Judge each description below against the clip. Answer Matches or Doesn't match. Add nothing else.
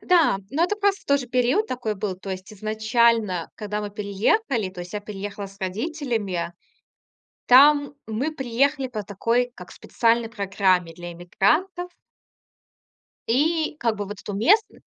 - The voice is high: Matches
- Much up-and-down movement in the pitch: Matches